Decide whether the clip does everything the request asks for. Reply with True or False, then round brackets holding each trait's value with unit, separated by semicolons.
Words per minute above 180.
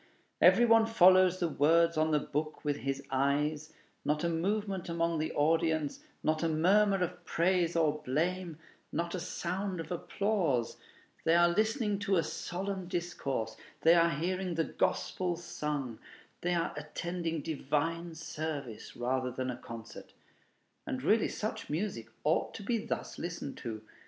False (150 wpm)